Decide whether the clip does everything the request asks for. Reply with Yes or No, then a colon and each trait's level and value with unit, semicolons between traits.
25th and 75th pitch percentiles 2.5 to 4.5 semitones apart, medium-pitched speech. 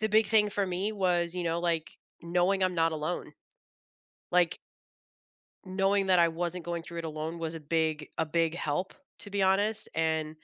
Yes: average, 2.8 semitones; medium, 175 Hz